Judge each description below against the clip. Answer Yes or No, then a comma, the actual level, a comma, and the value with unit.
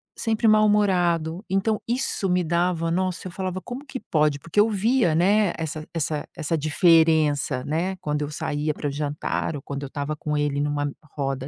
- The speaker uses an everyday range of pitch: Yes, average, 4.3 semitones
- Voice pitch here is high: No, medium, 165 Hz